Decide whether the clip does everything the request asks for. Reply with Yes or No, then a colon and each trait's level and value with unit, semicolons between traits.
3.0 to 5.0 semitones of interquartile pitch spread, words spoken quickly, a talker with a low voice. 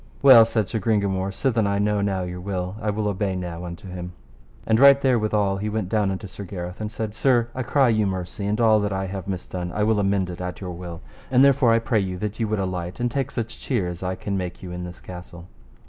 Yes: average, 3.4 semitones; fast, 250 wpm; low, 100 Hz